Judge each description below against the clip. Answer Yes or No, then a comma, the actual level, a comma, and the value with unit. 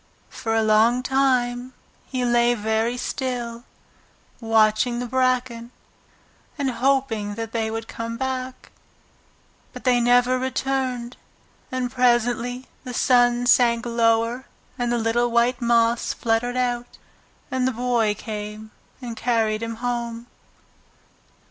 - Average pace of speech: No, slow, 120 wpm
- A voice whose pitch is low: No, high, 240 Hz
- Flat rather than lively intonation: Yes, narrow, 1.7 semitones